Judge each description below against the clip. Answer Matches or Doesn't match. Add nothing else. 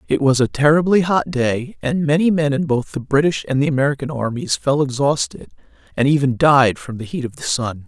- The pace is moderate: Doesn't match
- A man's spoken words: Doesn't match